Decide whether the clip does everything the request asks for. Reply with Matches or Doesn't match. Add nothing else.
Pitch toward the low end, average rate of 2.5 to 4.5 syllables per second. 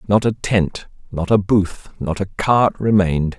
Matches